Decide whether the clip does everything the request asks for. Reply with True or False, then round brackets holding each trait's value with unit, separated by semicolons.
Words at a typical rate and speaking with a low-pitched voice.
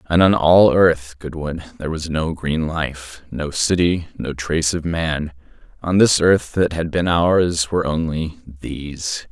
True (160 wpm; 80 Hz)